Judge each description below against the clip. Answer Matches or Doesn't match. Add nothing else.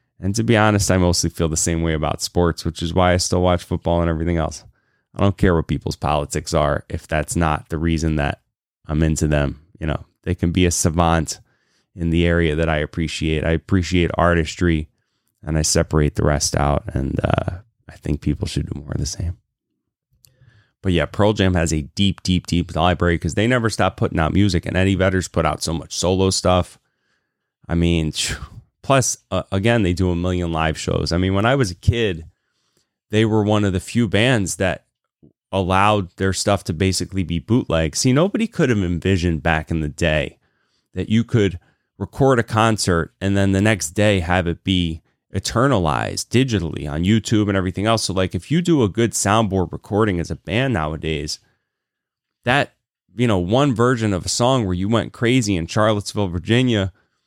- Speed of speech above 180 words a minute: Matches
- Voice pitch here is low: Matches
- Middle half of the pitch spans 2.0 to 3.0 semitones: Doesn't match